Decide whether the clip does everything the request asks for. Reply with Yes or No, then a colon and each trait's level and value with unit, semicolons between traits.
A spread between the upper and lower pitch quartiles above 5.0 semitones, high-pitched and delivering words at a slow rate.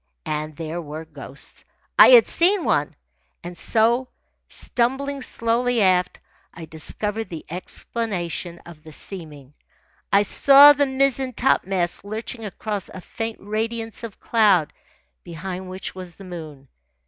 Yes: wide, 5.6 semitones; high, 195 Hz; slow, 130 wpm